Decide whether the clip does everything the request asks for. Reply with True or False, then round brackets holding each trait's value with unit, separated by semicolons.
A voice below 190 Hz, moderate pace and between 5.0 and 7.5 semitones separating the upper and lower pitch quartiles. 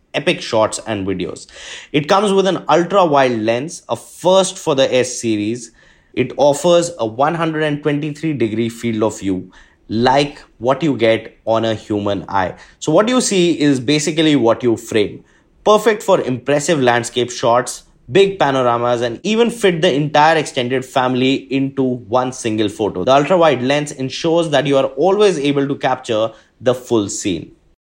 True (135 Hz; 160 wpm; 5.6 semitones)